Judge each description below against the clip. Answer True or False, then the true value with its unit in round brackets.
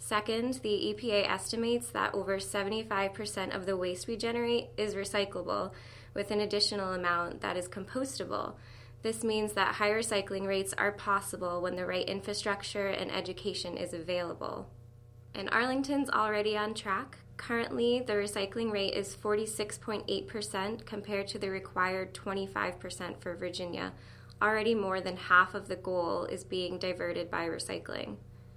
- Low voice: False (195 Hz)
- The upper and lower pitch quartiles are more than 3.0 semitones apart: False (2.7 semitones)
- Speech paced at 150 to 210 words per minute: False (140 wpm)